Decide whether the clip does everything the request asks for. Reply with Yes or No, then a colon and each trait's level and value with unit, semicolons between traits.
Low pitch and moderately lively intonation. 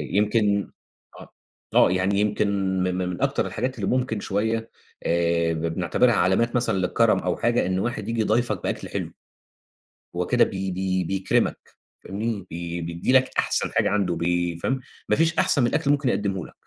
Yes: low, 100 Hz; average, 4.1 semitones